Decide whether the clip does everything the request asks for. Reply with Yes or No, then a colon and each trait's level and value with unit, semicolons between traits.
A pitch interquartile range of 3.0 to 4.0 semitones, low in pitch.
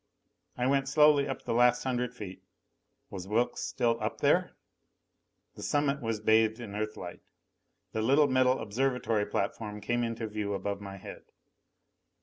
Yes: average, 3.6 semitones; low, 115 Hz